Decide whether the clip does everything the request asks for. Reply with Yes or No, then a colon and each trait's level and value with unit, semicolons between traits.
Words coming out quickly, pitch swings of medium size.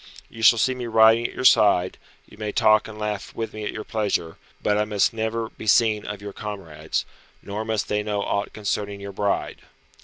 No: fast, 210 wpm; narrow, 1.4 semitones